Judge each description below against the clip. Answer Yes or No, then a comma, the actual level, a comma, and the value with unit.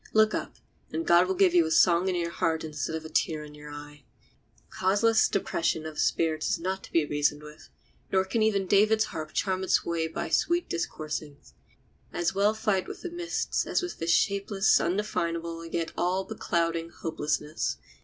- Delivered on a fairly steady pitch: No, average, 3.8 semitones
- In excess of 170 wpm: Yes, average, 185 wpm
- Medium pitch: Yes, medium, 170 Hz